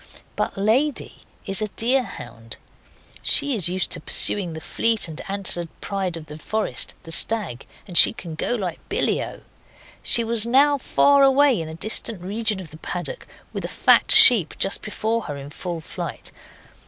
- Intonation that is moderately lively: No, wide, 5.8 semitones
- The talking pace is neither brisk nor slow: Yes, average, 175 wpm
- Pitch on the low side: No, high, 200 Hz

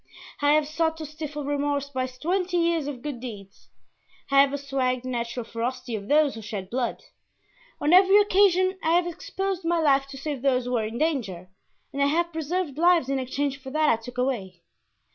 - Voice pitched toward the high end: Yes, very high, 280 Hz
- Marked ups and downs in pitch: No, average, 4.3 semitones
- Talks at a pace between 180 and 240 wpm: Yes, average, 200 wpm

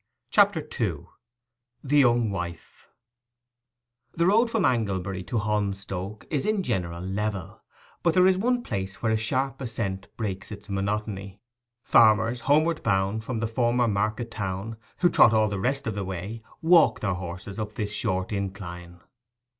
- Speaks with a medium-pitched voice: No, low, 110 Hz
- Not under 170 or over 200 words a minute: No, average, 150 wpm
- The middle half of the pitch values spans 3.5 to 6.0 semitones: Yes, average, 3.9 semitones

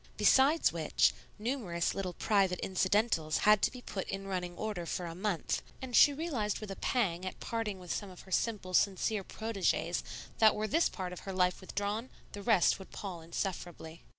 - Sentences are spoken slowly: No, average, 185 wpm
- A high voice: Yes, high, 195 Hz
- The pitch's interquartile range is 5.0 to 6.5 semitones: No, average, 3.3 semitones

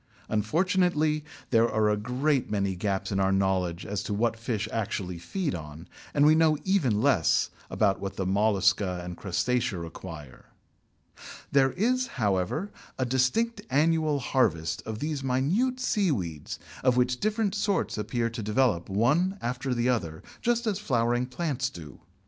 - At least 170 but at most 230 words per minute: No, average, 150 wpm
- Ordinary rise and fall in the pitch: No, wide, 7.7 semitones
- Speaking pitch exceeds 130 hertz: No, low, 120 Hz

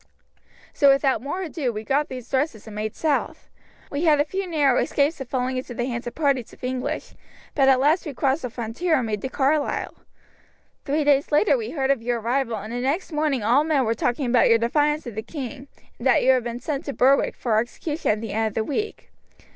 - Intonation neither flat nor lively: Yes, average, 3.7 semitones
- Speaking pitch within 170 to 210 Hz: No, very high, 265 Hz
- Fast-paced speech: Yes, fast, 230 wpm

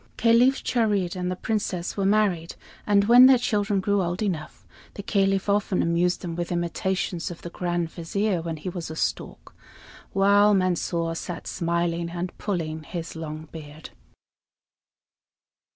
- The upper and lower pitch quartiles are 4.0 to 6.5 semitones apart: No, average, 3.1 semitones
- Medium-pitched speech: Yes, medium, 180 Hz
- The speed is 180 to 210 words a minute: No, average, 150 wpm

